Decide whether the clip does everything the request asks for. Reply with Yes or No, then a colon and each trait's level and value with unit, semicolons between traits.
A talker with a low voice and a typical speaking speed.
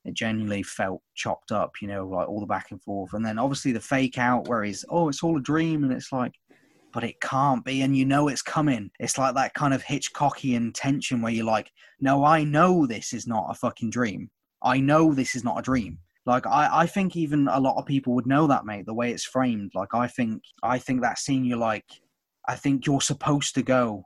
No: low, 130 Hz; fast, 240 wpm